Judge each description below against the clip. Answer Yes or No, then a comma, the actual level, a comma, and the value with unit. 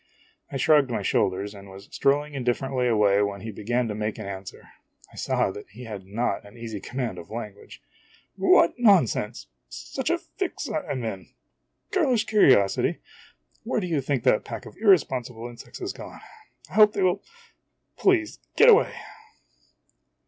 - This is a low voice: Yes, low, 120 Hz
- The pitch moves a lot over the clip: Yes, wide, 7.2 semitones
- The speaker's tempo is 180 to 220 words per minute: No, average, 170 wpm